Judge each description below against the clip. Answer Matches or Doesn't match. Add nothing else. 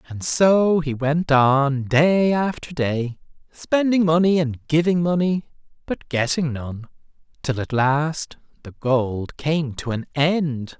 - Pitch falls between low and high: Matches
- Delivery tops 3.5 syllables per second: Doesn't match